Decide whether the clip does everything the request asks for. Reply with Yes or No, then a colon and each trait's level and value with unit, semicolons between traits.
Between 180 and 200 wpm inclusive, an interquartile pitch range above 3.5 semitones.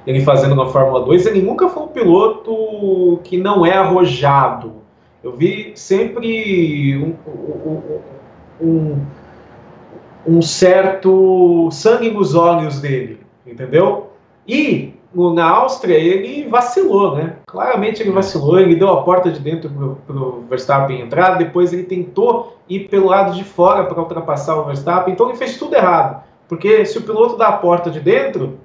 No: average, 150 wpm; average, 4.3 semitones